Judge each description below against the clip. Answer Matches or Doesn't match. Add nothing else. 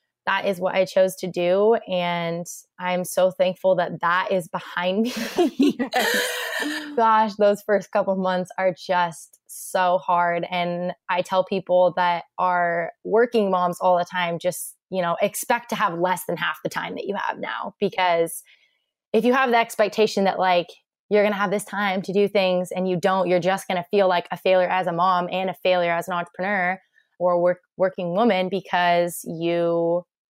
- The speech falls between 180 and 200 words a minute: Matches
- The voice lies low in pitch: Doesn't match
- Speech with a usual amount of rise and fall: Doesn't match